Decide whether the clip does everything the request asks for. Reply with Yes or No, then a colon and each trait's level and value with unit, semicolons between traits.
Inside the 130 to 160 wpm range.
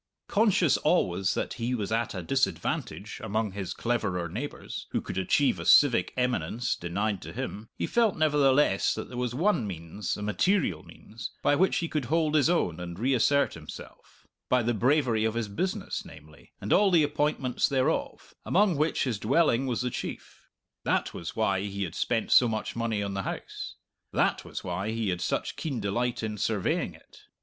No: average, 185 wpm